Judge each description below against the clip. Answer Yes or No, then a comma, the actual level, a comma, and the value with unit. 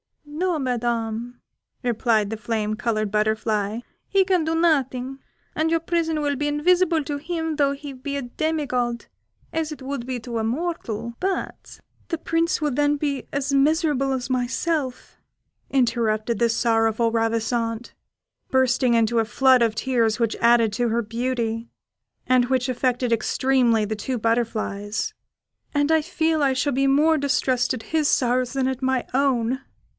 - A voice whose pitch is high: Yes, very high, 255 Hz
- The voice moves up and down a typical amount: Yes, average, 4.1 semitones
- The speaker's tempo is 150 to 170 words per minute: Yes, average, 160 wpm